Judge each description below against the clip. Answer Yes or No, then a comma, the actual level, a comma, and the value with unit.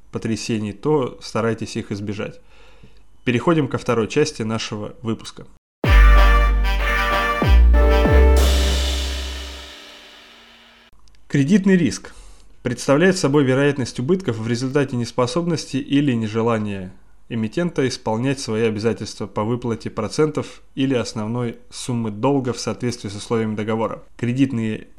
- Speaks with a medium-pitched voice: No, low, 115 Hz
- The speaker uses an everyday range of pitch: Yes, average, 3.8 semitones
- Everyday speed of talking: No, slow, 95 wpm